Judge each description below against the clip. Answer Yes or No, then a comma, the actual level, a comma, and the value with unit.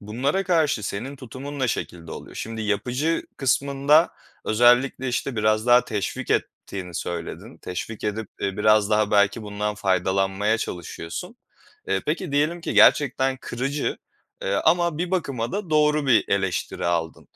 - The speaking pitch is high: No, low, 120 Hz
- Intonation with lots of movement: Yes, wide, 5.8 semitones